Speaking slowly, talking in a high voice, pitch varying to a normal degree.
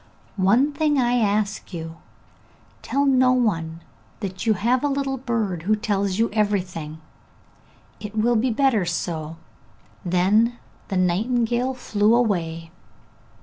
Yes: slow, 125 wpm; high, 215 Hz; average, 5.0 semitones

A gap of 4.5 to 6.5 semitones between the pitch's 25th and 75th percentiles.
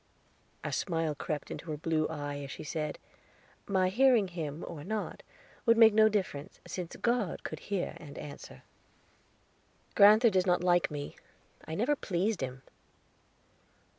Yes: wide, 5.6 semitones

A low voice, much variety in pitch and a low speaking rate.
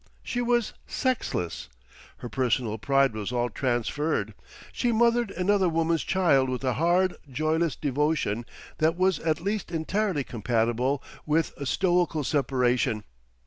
No: medium, 150 Hz; wide, 6.3 semitones; slow, 130 wpm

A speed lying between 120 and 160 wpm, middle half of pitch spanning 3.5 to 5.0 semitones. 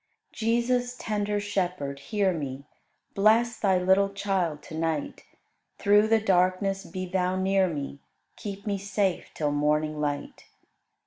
Yes: slow, 135 wpm; average, 4.3 semitones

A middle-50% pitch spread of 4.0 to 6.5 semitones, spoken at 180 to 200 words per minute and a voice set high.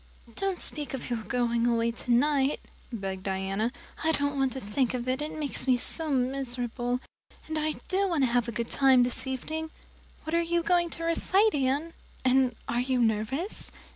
Yes: average, 4.5 semitones; average, 185 wpm; very high, 265 Hz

